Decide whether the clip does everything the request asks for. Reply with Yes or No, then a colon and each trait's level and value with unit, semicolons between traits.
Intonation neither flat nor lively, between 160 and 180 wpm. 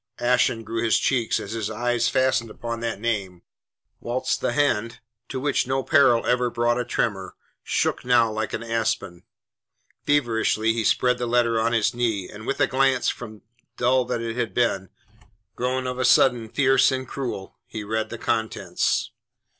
No: narrow, 2.1 semitones; average, 170 wpm